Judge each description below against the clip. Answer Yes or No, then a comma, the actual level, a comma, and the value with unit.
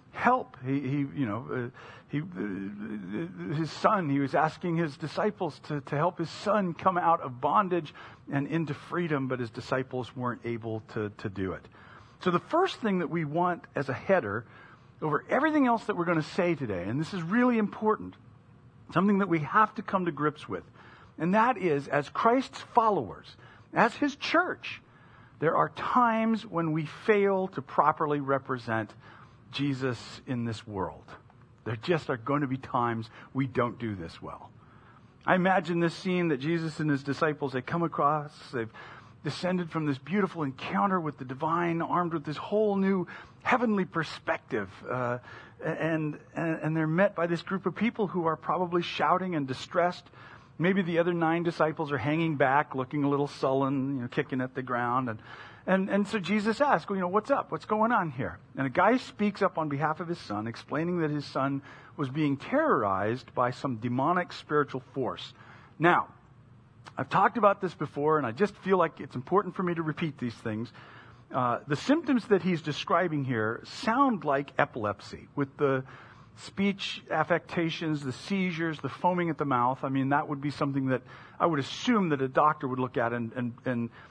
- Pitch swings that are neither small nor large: No, wide, 5.7 semitones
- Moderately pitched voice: Yes, medium, 150 Hz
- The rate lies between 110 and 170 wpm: No, average, 185 wpm